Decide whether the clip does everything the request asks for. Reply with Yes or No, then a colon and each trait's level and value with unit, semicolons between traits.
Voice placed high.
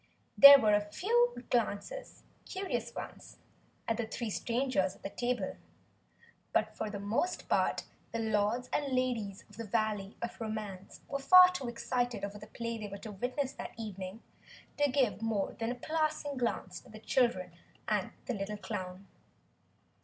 Yes: high, 230 Hz